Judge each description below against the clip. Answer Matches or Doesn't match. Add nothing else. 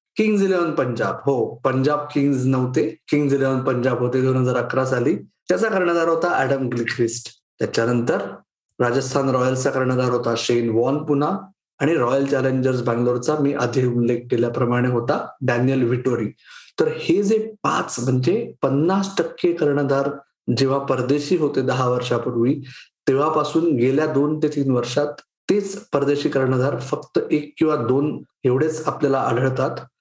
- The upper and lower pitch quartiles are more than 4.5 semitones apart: Doesn't match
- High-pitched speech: Doesn't match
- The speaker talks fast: Matches